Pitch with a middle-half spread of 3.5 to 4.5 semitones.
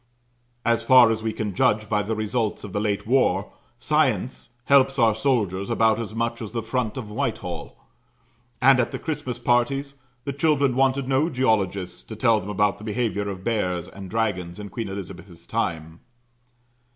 Yes: average, 3.9 semitones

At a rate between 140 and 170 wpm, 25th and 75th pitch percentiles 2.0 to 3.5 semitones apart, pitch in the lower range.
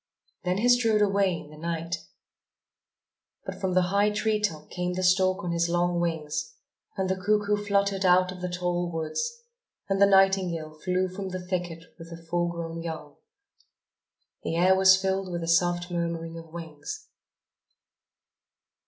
No: average, 160 wpm; narrow, 2.5 semitones; medium, 180 Hz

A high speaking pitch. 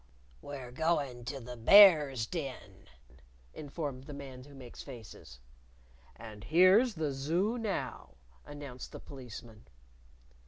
No: medium, 140 Hz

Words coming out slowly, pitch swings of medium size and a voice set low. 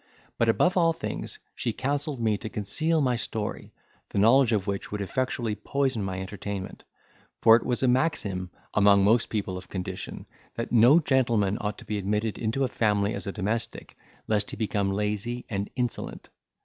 No: average, 175 wpm; average, 3.5 semitones; low, 110 Hz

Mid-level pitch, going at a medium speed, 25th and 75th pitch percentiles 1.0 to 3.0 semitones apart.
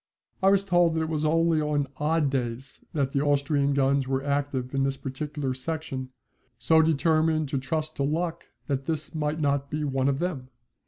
Yes: medium, 145 Hz; average, 190 wpm; average, 2.7 semitones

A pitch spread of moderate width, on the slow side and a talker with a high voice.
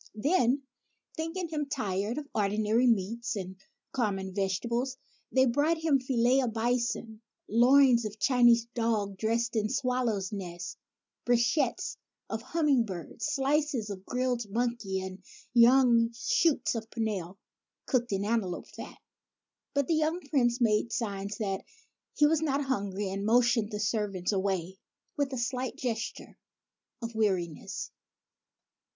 Yes: average, 4.2 semitones; slow, 130 wpm; high, 235 Hz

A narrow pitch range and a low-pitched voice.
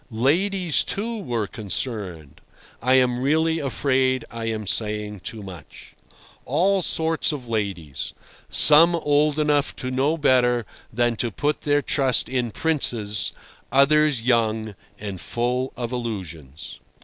No: average, 5.3 semitones; low, 125 Hz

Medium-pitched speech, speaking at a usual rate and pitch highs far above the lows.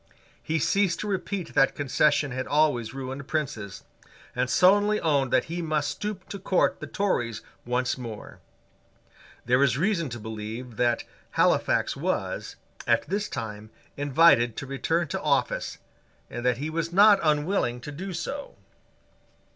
Yes: medium, 145 Hz; average, 145 wpm; wide, 6.0 semitones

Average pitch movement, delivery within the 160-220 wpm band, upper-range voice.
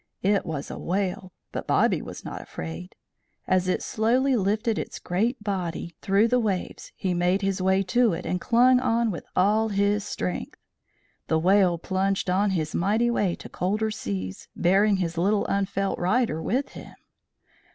Yes: average, 3.3 semitones; average, 165 wpm; high, 195 Hz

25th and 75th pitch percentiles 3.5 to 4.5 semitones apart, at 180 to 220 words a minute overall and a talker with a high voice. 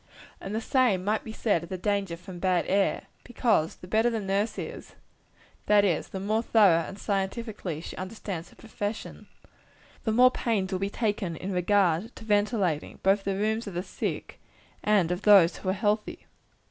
No: average, 2.8 semitones; average, 185 wpm; high, 200 Hz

